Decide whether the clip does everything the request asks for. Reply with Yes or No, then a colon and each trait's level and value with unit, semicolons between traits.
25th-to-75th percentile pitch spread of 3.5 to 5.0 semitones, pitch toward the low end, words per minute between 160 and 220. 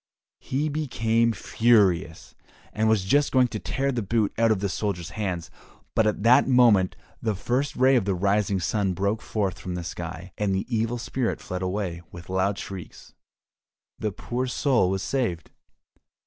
Yes: average, 4.1 semitones; low, 105 Hz; average, 170 wpm